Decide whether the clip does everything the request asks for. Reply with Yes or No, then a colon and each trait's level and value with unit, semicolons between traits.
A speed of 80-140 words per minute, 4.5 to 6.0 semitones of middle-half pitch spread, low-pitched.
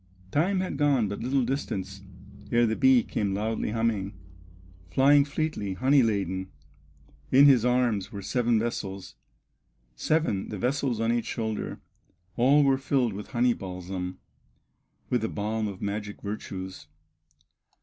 Yes: slow, 135 wpm; average, 4.8 semitones; low, 115 Hz